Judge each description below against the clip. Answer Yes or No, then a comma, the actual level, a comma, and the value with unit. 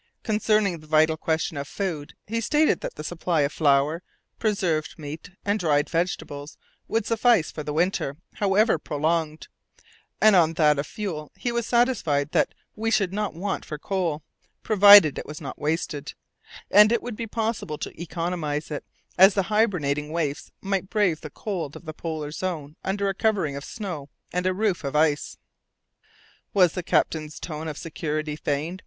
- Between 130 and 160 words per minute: No, average, 170 wpm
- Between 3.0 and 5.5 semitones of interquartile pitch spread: Yes, average, 5.0 semitones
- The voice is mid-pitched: Yes, medium, 165 Hz